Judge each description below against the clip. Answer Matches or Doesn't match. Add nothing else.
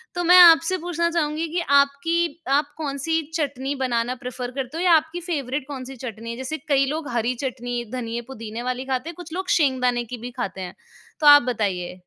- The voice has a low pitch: Doesn't match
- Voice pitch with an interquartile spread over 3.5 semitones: Matches